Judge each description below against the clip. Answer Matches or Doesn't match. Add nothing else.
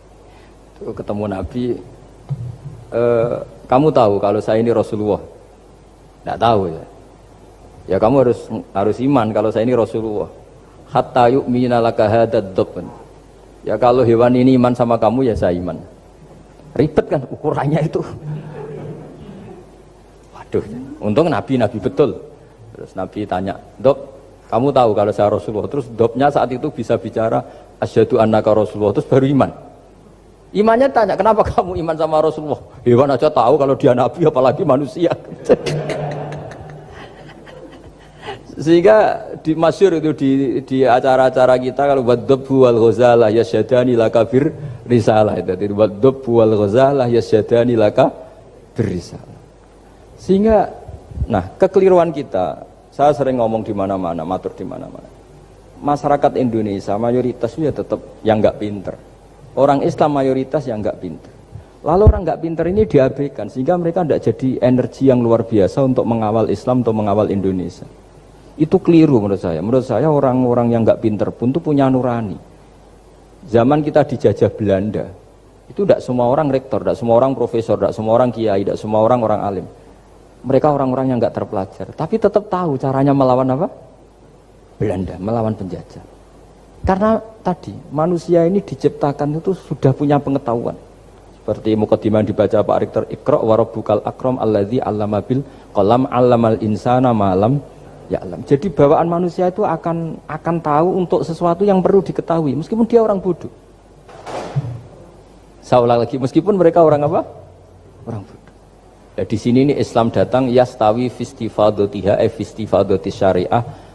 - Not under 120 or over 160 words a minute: Matches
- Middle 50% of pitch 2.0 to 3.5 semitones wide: Doesn't match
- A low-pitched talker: Matches